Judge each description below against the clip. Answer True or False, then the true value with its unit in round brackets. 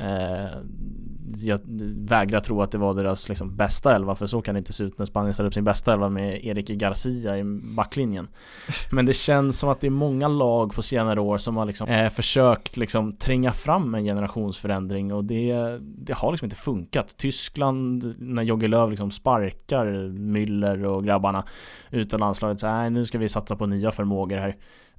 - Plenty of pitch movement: False (2.7 semitones)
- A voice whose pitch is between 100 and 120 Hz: True (105 Hz)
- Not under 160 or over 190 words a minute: True (185 wpm)